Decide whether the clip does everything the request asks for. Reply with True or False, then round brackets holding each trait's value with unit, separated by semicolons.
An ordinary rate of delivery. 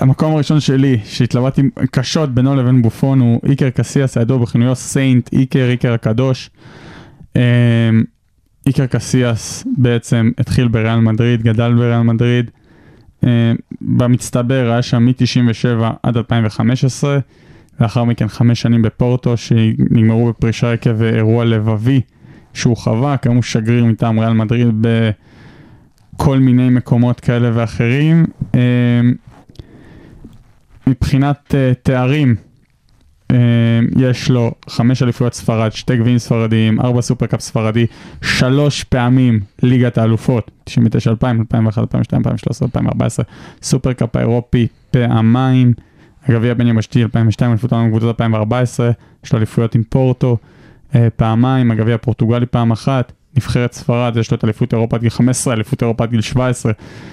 True (125 wpm)